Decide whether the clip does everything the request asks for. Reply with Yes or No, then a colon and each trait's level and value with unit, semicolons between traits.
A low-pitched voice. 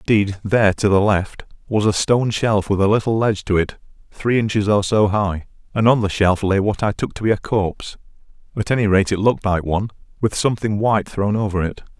Yes: low, 105 Hz